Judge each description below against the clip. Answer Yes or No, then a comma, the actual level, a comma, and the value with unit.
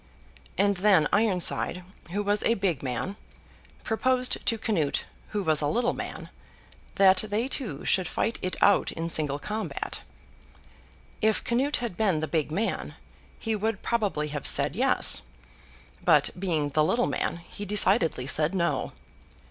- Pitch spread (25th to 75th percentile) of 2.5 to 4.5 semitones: No, wide, 5.6 semitones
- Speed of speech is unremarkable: Yes, average, 150 wpm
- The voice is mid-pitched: No, high, 195 Hz